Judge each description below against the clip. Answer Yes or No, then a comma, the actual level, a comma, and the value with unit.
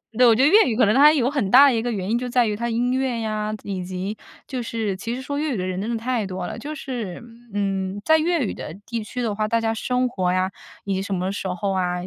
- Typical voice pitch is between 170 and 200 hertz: No, high, 225 Hz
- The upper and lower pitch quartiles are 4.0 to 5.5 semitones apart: Yes, average, 4.4 semitones